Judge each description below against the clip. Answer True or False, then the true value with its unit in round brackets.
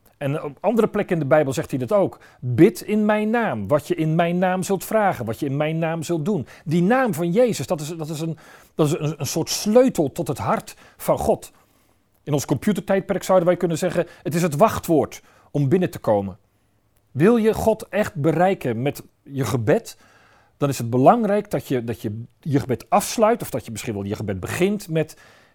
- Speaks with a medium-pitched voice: True (160 Hz)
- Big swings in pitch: True (5.7 semitones)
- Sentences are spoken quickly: True (215 wpm)